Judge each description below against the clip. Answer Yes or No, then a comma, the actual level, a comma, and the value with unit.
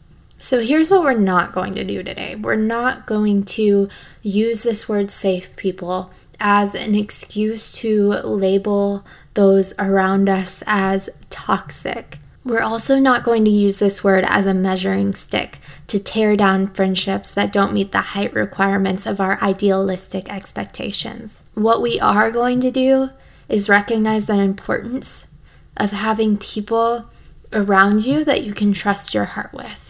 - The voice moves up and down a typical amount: No, narrow, 2.3 semitones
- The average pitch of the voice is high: Yes, high, 205 Hz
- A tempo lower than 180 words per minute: Yes, average, 155 wpm